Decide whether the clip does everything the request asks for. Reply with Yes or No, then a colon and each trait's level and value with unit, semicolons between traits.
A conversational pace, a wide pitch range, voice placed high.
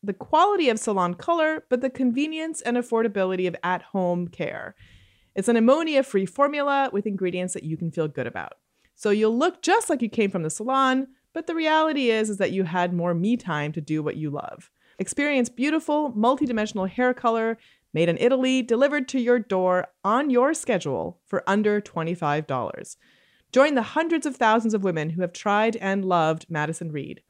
Yes: average, 180 wpm; wide, 6.8 semitones; high, 220 Hz